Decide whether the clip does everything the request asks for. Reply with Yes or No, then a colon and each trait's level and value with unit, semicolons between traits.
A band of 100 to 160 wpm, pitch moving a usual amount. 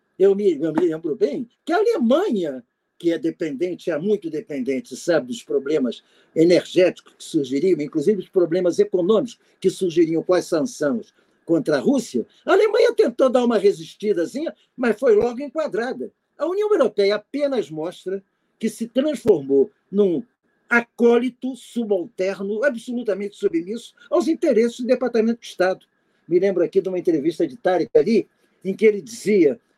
No: average, 150 wpm; wide, 6.8 semitones